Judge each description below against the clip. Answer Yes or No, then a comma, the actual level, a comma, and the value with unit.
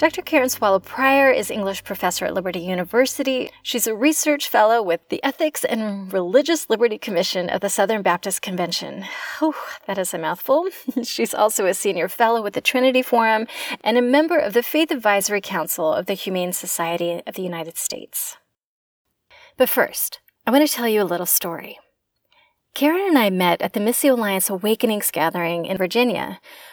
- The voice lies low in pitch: No, high, 220 Hz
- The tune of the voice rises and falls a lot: Yes, wide, 6.4 semitones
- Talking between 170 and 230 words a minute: Yes, average, 175 wpm